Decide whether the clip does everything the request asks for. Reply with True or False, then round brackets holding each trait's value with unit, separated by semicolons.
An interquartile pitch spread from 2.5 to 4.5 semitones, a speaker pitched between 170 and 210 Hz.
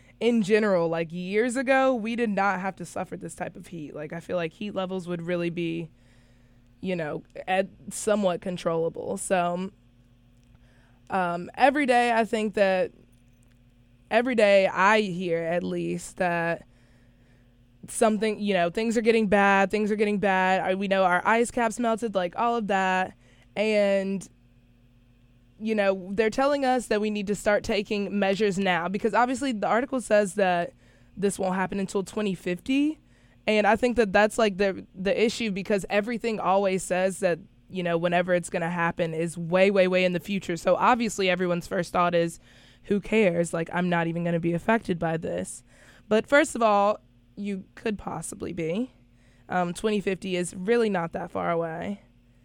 True (4.0 semitones; 185 Hz)